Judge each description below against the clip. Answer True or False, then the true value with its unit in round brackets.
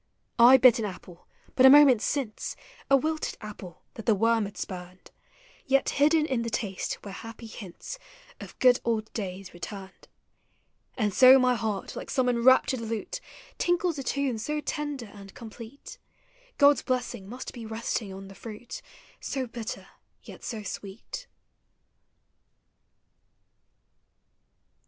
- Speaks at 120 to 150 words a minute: True (140 wpm)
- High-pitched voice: True (230 Hz)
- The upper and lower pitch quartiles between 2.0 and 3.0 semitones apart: False (4.2 semitones)